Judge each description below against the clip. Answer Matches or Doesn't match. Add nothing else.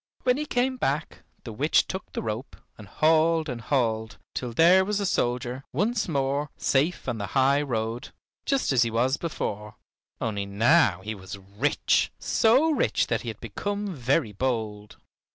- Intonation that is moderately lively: Doesn't match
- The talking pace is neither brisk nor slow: Matches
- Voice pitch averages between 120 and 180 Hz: Matches